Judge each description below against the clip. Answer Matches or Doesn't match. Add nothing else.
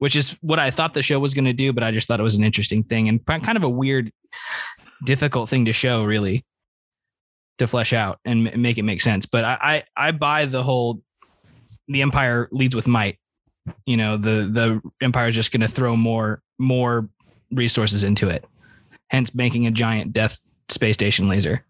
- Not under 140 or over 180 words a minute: Doesn't match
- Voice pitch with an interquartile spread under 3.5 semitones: Matches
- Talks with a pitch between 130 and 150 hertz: Doesn't match